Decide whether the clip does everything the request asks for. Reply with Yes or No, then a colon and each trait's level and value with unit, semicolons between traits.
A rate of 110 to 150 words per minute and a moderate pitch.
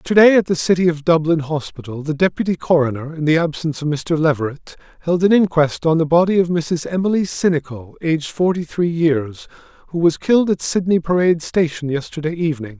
No: average, 185 wpm; medium, 160 Hz